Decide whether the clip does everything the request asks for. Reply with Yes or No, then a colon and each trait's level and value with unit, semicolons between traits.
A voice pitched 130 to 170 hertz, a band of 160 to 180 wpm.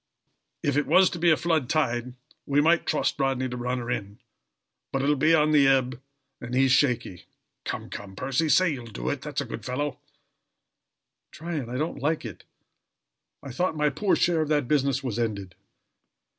No: low, 135 Hz; average, 195 wpm